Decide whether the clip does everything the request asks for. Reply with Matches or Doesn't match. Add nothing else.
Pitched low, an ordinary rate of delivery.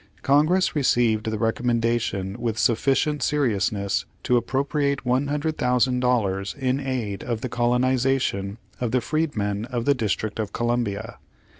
Doesn't match